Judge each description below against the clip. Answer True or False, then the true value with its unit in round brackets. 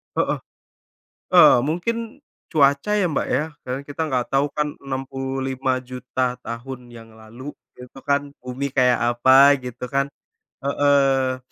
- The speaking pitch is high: False (135 Hz)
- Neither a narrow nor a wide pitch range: False (2.0 semitones)